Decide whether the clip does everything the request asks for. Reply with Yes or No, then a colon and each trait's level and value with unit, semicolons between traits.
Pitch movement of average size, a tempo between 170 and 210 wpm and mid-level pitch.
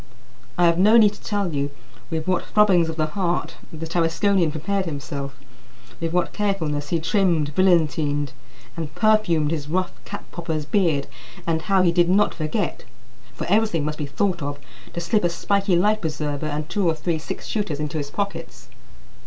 Yes: average, 4.2 semitones; average, 180 wpm; medium, 170 Hz